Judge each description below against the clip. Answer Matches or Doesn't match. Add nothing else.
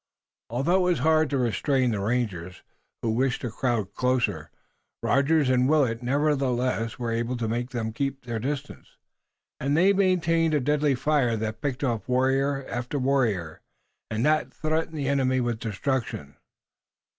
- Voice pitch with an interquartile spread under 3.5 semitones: Doesn't match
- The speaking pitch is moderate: Doesn't match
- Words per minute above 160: Doesn't match